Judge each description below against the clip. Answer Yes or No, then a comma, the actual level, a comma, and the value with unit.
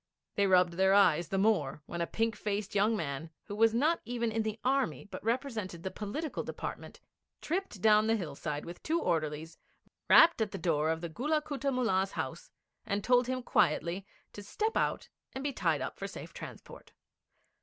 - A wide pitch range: Yes, wide, 6.3 semitones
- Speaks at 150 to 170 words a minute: No, average, 185 wpm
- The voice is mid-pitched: No, high, 210 Hz